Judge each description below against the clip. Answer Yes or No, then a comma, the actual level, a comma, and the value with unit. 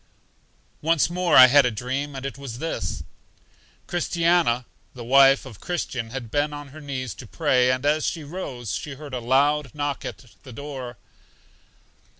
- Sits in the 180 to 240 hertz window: No, low, 135 Hz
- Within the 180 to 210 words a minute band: No, average, 165 wpm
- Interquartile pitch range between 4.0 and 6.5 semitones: No, average, 3.0 semitones